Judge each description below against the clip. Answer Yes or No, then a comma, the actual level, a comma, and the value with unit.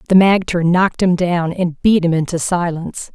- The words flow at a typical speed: Yes, average, 190 wpm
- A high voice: No, medium, 175 Hz